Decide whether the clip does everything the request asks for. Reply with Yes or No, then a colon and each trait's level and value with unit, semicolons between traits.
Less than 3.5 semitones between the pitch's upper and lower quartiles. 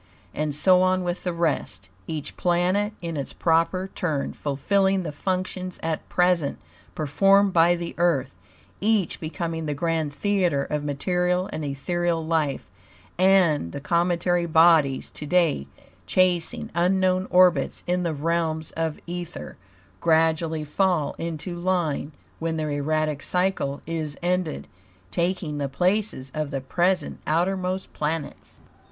Yes: average, 3.1 semitones